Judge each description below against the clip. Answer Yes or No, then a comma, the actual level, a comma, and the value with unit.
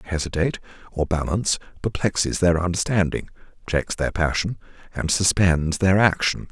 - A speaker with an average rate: No, slow, 130 wpm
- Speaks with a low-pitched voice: Yes, very low, 90 Hz